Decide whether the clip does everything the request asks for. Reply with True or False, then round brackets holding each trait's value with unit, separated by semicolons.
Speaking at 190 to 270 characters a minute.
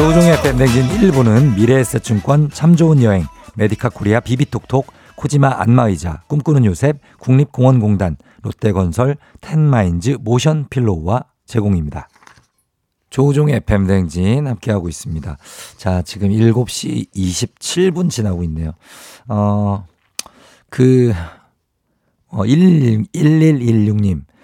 True (240 characters per minute)